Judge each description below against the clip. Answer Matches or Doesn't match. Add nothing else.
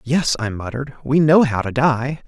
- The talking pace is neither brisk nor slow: Doesn't match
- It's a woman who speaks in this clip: Doesn't match